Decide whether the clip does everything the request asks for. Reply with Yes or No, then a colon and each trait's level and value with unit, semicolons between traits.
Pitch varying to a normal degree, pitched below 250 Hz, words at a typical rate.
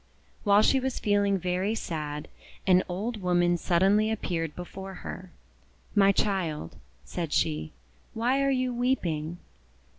No: average, 3.8 semitones; high, 190 Hz; slow, 125 wpm